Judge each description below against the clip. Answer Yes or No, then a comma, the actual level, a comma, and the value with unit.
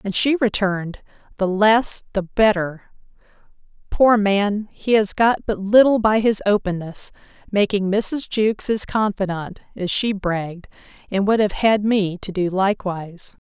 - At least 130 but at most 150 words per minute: Yes, average, 145 wpm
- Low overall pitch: No, high, 200 Hz